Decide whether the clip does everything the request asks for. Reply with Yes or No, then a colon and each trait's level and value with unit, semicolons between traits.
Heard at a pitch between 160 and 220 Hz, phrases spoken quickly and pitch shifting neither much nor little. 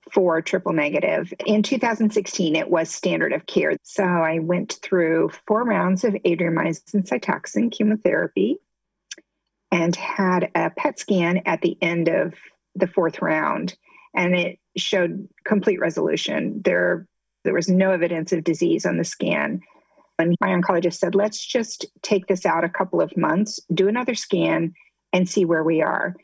No: medium, 185 Hz; average, 155 wpm; average, 3.3 semitones